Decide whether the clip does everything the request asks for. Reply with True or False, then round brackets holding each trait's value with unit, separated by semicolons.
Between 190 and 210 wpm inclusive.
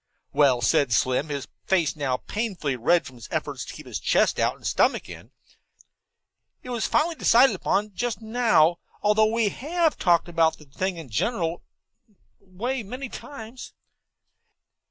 False (155 wpm)